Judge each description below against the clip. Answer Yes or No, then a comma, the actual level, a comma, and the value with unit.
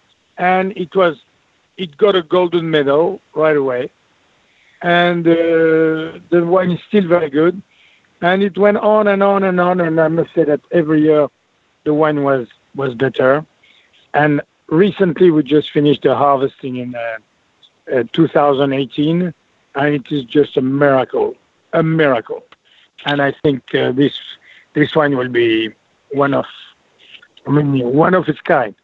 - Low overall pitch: No, medium, 155 Hz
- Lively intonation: No, average, 3.8 semitones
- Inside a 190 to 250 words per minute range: No, average, 155 wpm